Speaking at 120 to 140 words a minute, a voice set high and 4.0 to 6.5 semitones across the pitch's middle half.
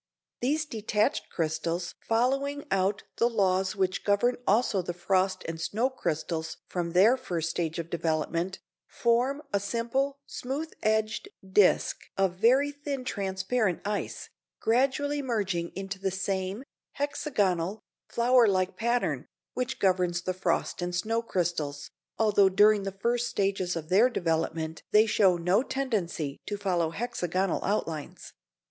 Yes: slow, 135 wpm; high, 195 Hz; average, 5.0 semitones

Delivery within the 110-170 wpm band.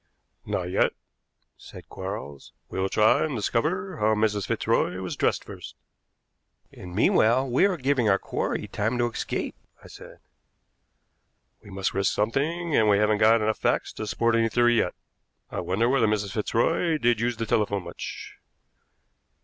Yes: average, 160 wpm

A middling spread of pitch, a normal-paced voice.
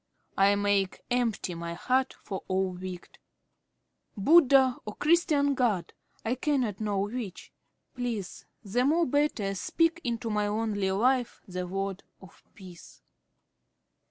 No: average, 5.0 semitones; slow, 130 wpm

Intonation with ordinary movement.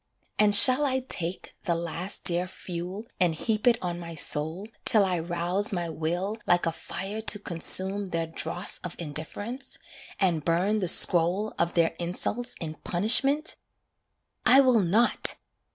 Yes: average, 3.9 semitones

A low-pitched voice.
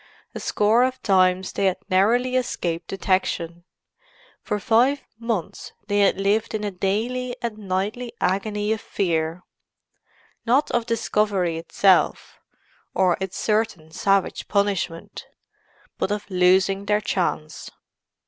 No: high, 200 Hz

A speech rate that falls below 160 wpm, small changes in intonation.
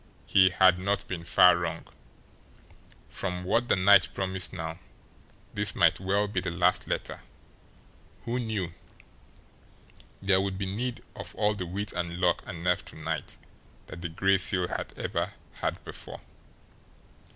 Yes: average, 150 wpm; narrow, 2.0 semitones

